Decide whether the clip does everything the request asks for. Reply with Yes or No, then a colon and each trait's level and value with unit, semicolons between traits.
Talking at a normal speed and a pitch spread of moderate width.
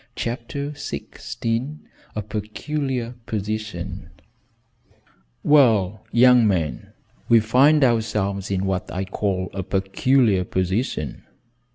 No: slow, 90 wpm; average, 4.5 semitones